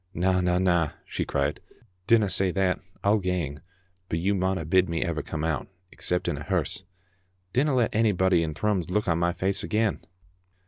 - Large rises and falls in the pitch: No, average, 2.9 semitones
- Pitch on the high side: No, very low, 90 Hz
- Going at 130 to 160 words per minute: No, average, 180 wpm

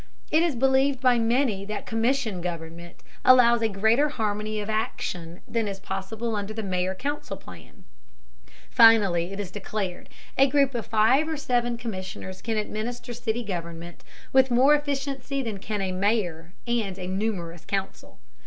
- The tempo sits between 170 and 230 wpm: No, average, 155 wpm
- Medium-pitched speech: No, high, 220 Hz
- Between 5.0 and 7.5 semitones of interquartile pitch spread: No, average, 4.5 semitones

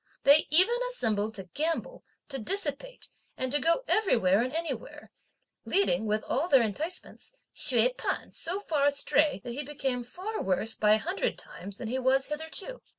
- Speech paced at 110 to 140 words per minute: No, average, 165 wpm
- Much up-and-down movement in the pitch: Yes, wide, 6.7 semitones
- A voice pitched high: Yes, very high, 280 Hz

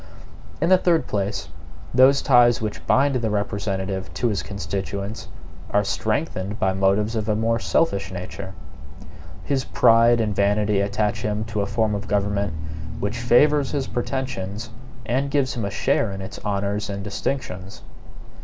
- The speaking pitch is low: Yes, low, 105 Hz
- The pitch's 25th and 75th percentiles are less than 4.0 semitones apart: Yes, average, 3.3 semitones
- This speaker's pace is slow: No, average, 155 wpm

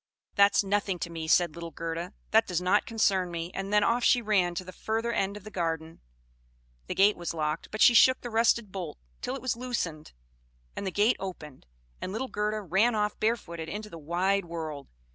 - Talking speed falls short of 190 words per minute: No, fast, 205 wpm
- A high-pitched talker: Yes, high, 195 Hz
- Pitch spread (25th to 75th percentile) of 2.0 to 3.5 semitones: No, average, 4.2 semitones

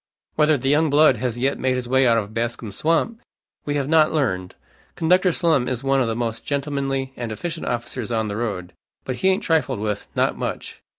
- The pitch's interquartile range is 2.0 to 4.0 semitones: No, average, 4.7 semitones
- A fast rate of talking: Yes, fast, 210 wpm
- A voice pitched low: Yes, low, 130 Hz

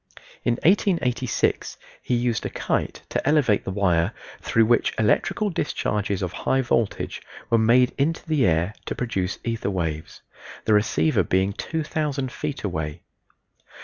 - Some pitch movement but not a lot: No, wide, 5.7 semitones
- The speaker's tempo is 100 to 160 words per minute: Yes, average, 140 wpm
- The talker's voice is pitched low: Yes, low, 115 Hz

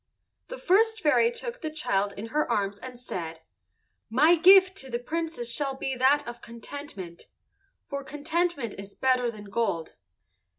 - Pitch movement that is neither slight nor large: No, wide, 6.3 semitones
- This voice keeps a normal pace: Yes, average, 155 wpm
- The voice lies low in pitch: No, very high, 265 Hz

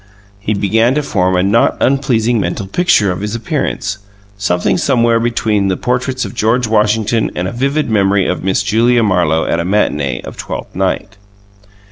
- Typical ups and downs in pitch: Yes, average, 3.7 semitones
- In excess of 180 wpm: No, average, 170 wpm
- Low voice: Yes, low, 110 Hz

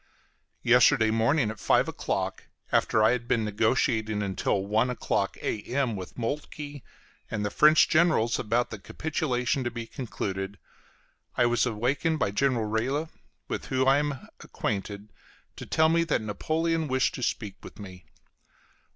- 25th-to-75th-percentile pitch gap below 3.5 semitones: No, average, 4.8 semitones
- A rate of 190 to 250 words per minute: No, average, 150 wpm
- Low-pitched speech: Yes, low, 120 Hz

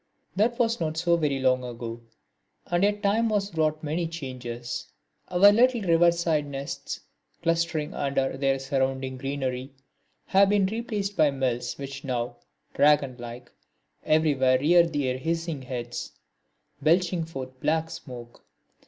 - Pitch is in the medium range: Yes, medium, 150 Hz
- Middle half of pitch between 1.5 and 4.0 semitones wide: No, average, 4.7 semitones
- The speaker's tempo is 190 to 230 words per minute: No, slow, 135 wpm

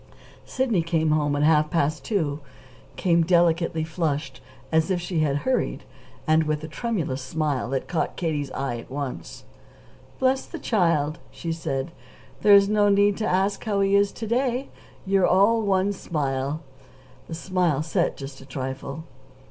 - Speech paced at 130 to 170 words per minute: Yes, average, 155 wpm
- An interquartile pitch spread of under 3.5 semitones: No, average, 5.2 semitones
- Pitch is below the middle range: No, medium, 165 Hz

